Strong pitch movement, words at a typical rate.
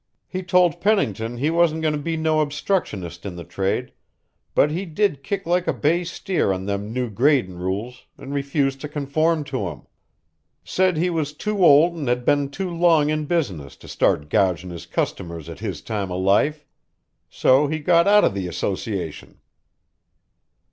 Yes: wide, 8.9 semitones; average, 175 wpm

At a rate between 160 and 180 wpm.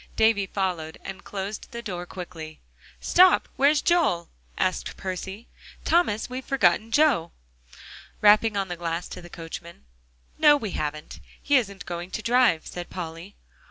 No: average, 145 wpm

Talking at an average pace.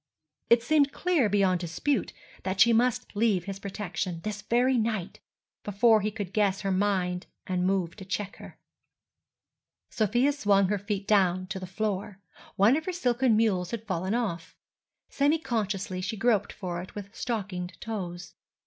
Yes: average, 160 wpm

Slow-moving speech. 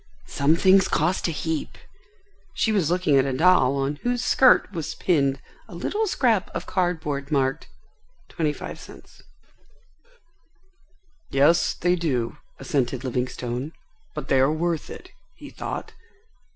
Yes: slow, 130 wpm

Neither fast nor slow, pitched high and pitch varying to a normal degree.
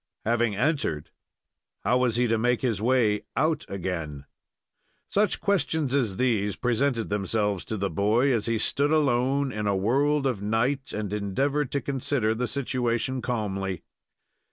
No: average, 150 wpm; low, 120 Hz; average, 4.7 semitones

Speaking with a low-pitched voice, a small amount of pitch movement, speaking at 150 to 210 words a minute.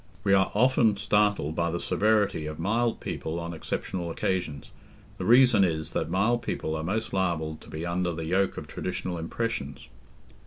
No: very low, 90 Hz; average, 4.4 semitones; average, 170 wpm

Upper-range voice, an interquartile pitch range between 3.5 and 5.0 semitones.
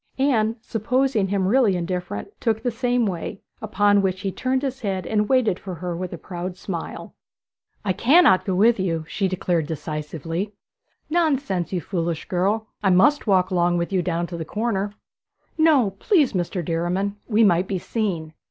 Yes: high, 195 Hz; average, 4.2 semitones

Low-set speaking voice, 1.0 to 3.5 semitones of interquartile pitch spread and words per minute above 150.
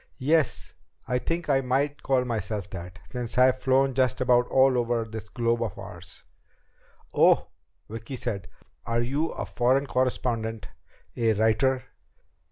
No: low, 125 Hz; average, 2.7 semitones; average, 140 wpm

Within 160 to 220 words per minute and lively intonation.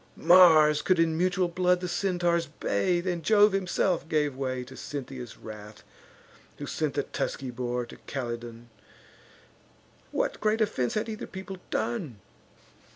No: average, 140 wpm; wide, 6.3 semitones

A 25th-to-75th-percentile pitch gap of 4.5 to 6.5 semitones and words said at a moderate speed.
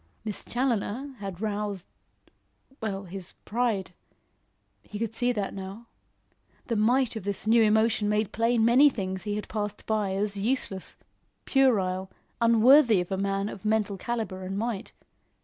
No: average, 2.8 semitones; average, 150 wpm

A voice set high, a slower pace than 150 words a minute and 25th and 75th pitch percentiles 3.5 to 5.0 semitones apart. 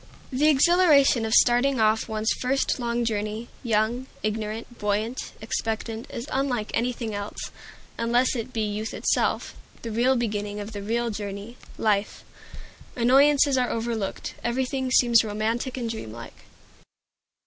No: high, 230 Hz; slow, 135 wpm; average, 2.7 semitones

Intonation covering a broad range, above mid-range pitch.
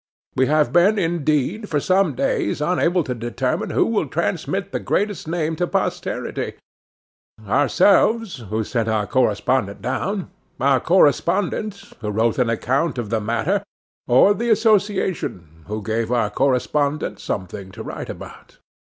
No: wide, 7.9 semitones; medium, 140 Hz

